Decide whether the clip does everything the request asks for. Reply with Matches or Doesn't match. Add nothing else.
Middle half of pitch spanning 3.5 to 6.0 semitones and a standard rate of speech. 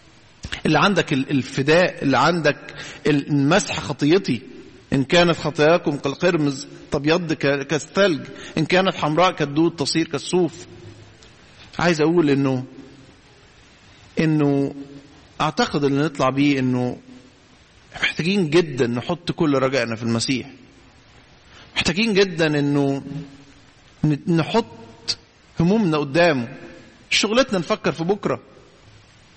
Doesn't match